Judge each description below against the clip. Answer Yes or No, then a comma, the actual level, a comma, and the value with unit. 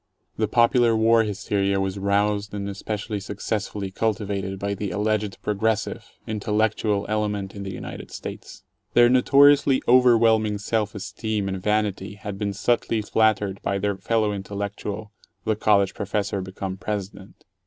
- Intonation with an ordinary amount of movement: No, narrow, 1.7 semitones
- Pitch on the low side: Yes, low, 105 Hz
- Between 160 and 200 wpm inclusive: No, slow, 135 wpm